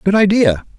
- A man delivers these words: Yes, male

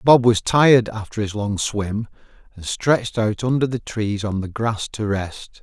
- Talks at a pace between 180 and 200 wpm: Yes, average, 190 wpm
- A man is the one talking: Yes, male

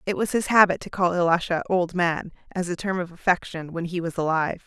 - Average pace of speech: No, fast, 230 wpm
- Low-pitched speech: No, medium, 175 Hz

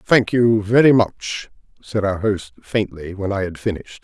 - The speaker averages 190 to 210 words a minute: No, average, 180 wpm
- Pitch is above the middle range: No, low, 105 Hz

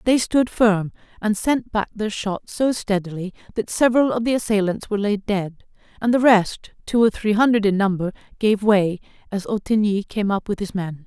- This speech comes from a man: No, female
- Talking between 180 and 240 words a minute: Yes, average, 195 wpm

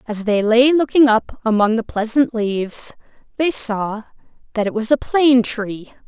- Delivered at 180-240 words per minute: No, average, 170 wpm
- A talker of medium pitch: No, high, 230 Hz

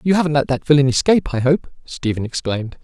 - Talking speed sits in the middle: No, fast, 210 wpm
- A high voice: No, medium, 140 Hz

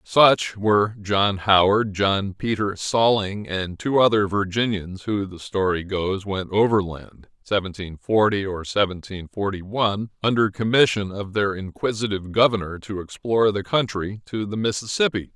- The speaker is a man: Yes, male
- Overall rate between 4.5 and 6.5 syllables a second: No, 4.0 syllables/s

